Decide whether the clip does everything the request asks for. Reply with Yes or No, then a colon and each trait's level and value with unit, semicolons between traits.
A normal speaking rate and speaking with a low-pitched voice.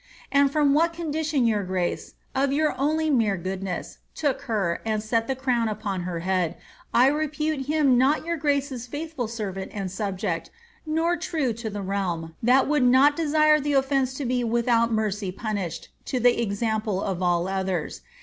No: average, 170 wpm; high, 235 Hz